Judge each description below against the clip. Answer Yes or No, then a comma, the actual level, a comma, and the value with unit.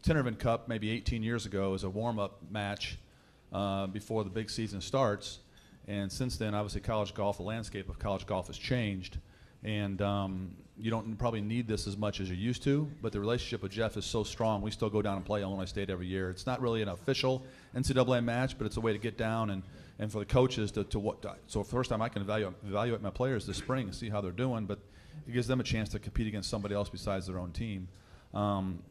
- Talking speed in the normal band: No, fast, 240 wpm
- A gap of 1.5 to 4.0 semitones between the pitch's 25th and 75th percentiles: Yes, average, 2.8 semitones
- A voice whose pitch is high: No, low, 105 Hz